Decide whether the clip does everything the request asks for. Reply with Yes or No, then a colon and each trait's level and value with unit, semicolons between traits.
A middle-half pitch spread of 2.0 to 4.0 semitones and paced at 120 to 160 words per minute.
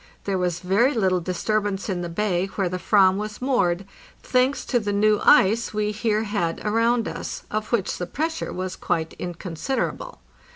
No: average, 3.6 semitones; average, 170 wpm